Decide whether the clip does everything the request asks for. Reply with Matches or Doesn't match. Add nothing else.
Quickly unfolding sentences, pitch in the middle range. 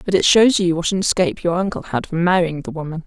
Matches